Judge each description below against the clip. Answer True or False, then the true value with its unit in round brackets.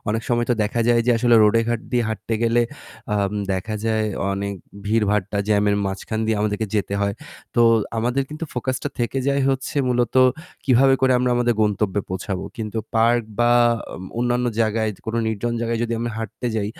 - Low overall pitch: True (115 Hz)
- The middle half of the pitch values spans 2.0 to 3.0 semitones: True (2.4 semitones)